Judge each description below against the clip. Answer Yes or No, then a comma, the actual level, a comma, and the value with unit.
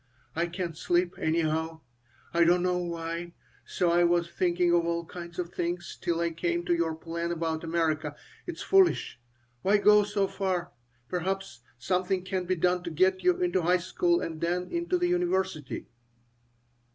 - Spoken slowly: No, average, 170 wpm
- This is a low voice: No, medium, 175 Hz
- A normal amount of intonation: No, narrow, 1.7 semitones